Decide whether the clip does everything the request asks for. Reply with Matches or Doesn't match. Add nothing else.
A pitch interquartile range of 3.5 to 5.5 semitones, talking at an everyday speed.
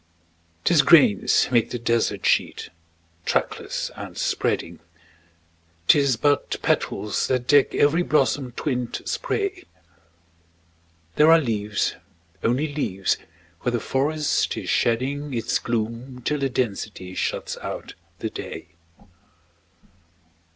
Doesn't match